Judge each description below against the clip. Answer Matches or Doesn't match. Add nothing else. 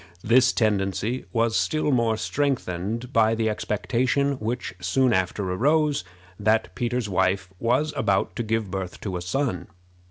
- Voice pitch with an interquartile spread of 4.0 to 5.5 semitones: Matches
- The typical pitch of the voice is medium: Doesn't match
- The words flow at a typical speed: Matches